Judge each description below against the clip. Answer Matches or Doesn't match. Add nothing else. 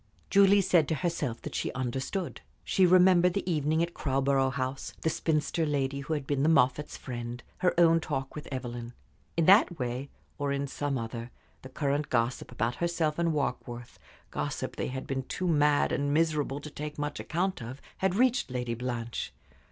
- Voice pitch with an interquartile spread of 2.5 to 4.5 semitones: Matches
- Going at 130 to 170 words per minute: Doesn't match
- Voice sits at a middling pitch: Matches